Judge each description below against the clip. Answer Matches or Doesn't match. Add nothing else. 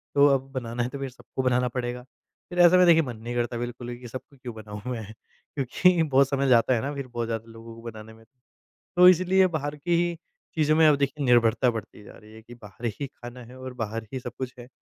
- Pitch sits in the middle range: Doesn't match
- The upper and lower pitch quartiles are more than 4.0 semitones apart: Doesn't match